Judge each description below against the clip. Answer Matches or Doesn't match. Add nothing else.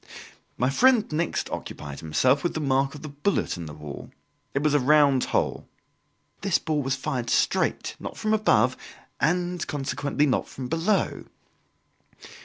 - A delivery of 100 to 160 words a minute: Matches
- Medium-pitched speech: Matches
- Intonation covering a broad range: Doesn't match